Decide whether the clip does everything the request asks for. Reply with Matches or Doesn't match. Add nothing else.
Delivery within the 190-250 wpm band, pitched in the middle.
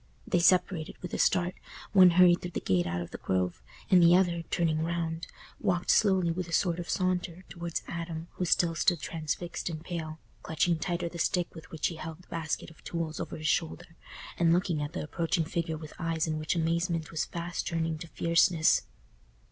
Matches